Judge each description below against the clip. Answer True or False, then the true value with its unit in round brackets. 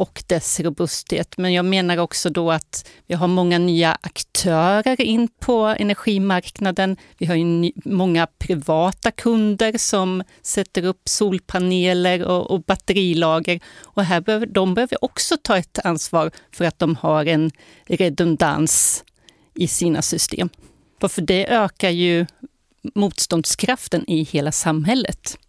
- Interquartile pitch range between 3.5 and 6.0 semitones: False (3.0 semitones)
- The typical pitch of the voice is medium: True (180 Hz)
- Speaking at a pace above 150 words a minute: False (130 wpm)